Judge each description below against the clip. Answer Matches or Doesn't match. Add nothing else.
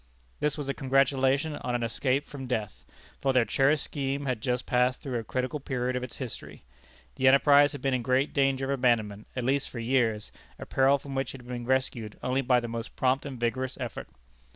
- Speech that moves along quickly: Matches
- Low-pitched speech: Matches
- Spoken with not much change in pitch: Matches